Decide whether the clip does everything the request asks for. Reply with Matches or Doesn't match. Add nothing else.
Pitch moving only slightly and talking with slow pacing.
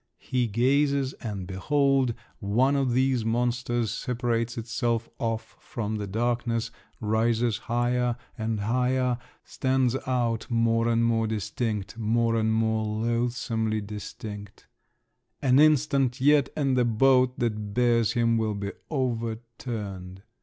Matches